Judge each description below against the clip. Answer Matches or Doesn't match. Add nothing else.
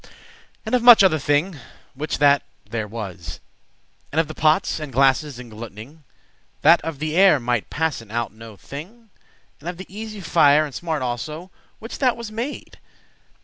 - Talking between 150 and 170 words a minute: Doesn't match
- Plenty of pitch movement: Matches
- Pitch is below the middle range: Doesn't match